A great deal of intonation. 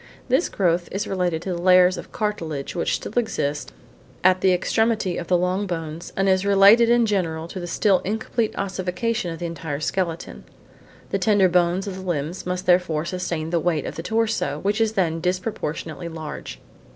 No: average, 3.0 semitones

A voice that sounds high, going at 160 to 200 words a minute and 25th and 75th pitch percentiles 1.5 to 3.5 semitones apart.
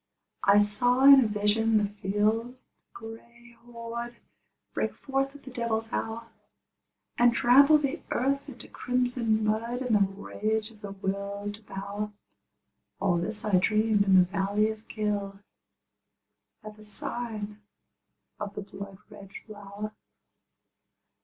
No: high, 215 Hz; slow, 135 wpm; narrow, 2.6 semitones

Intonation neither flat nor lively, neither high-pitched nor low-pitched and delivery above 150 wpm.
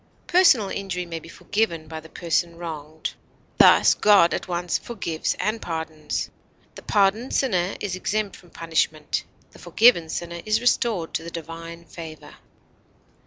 No: average, 4.0 semitones; medium, 170 Hz; average, 145 wpm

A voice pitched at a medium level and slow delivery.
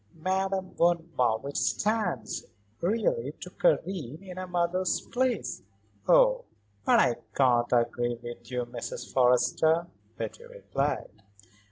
Yes: medium, 170 Hz; slow, 115 wpm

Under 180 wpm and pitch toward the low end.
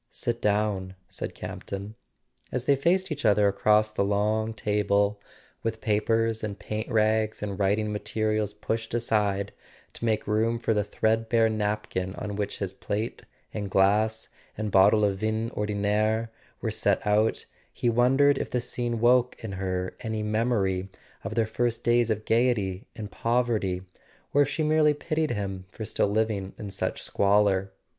Yes: average, 160 wpm; low, 110 Hz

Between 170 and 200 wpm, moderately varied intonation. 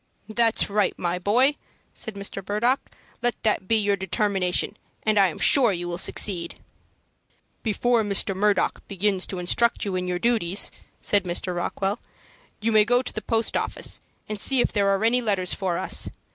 Yes: average, 175 wpm; average, 3.3 semitones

